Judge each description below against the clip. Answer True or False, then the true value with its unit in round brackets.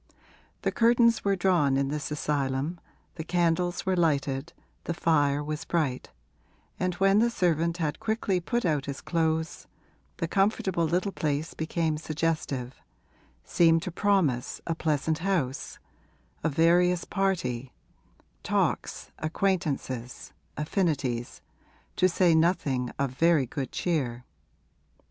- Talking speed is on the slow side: True (120 wpm)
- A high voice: False (165 Hz)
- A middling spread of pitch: True (4.0 semitones)